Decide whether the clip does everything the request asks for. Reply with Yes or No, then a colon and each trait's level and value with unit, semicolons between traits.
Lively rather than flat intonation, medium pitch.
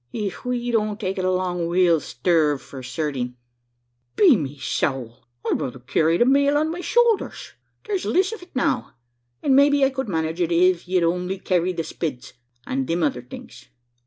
Yes: wide, 8.4 semitones; medium, 180 Hz